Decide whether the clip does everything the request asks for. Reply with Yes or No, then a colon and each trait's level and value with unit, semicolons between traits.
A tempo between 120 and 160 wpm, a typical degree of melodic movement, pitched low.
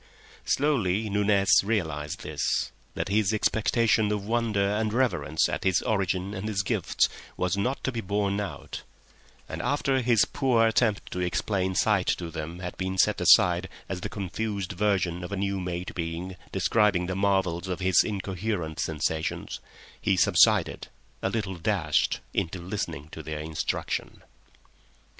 Yes: average, 150 wpm; average, 3.0 semitones; very low, 95 Hz